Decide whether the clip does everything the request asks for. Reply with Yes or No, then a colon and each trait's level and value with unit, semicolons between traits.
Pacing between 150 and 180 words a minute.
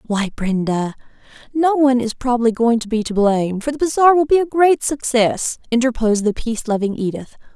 No: average, 190 wpm